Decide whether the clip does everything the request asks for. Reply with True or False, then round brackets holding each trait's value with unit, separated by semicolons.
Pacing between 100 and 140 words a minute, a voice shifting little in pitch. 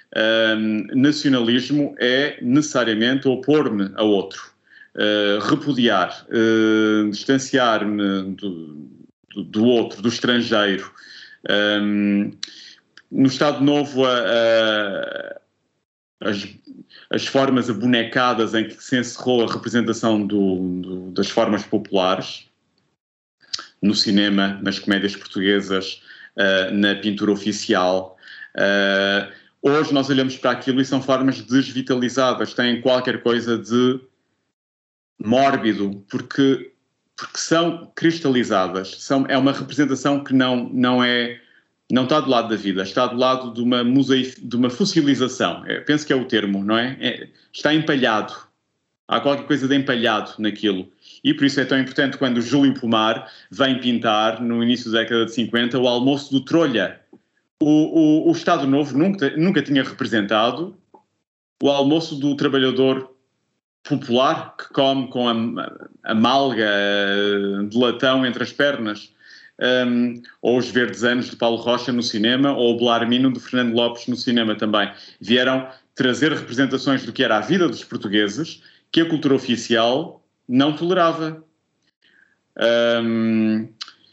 False (135 wpm; 4.0 semitones)